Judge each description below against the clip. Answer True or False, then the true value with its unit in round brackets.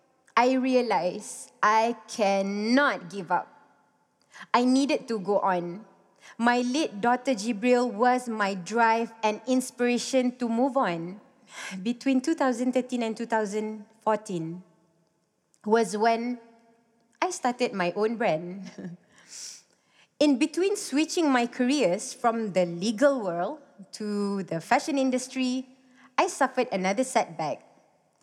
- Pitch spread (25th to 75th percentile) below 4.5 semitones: True (4.0 semitones)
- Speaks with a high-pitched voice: True (230 Hz)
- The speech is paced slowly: True (110 wpm)